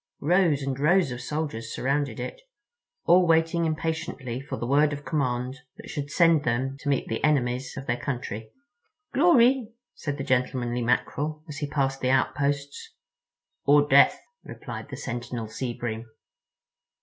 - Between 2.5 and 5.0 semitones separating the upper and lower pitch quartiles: Yes, average, 3.5 semitones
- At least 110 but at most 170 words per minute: Yes, average, 150 wpm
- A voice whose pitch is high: No, medium, 140 Hz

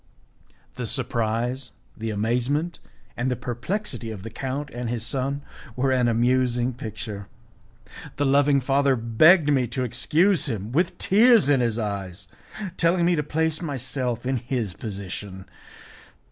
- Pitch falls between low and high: No, low, 125 Hz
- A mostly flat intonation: No, average, 3.9 semitones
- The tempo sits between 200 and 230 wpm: No, average, 140 wpm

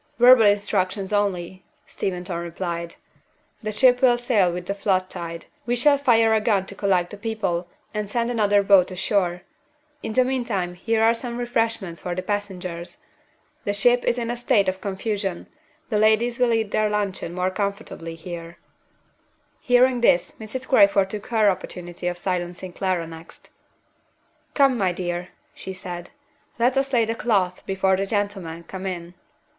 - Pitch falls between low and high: No, high, 200 Hz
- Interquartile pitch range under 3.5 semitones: No, average, 4.1 semitones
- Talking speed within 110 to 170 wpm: Yes, average, 160 wpm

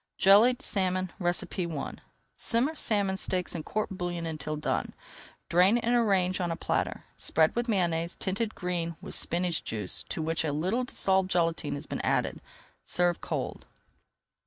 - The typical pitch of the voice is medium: Yes, medium, 180 Hz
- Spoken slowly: No, average, 150 wpm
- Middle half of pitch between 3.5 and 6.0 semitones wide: No, average, 3.1 semitones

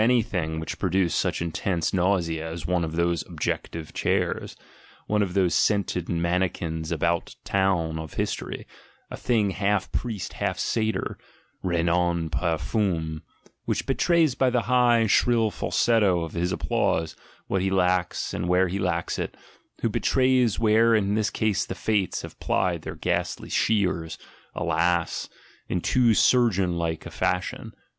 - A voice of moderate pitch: No, very low, 90 Hz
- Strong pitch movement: No, average, 4.2 semitones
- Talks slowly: No, average, 155 wpm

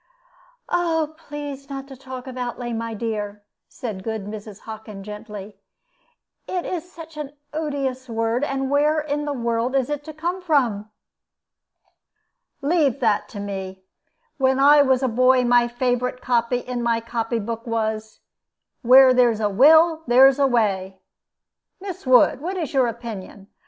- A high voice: Yes, very high, 250 Hz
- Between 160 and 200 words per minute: No, average, 150 wpm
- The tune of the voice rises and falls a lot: No, average, 4.2 semitones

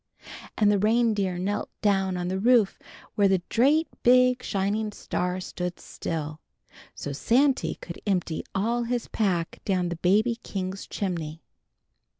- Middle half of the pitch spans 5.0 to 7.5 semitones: No, average, 4.3 semitones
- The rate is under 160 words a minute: Yes, average, 140 wpm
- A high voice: Yes, high, 195 Hz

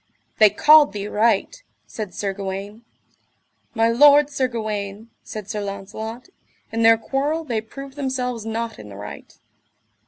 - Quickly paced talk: No, average, 145 wpm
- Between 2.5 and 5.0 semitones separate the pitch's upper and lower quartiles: Yes, average, 4.2 semitones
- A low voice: No, high, 225 Hz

